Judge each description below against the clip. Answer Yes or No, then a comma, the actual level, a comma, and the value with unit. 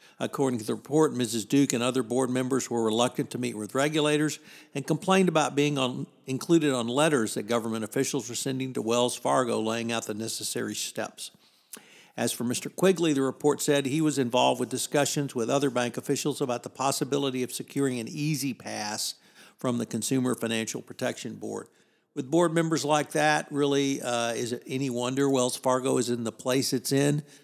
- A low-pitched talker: Yes, low, 130 Hz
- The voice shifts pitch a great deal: No, average, 3.0 semitones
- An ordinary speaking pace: Yes, average, 190 wpm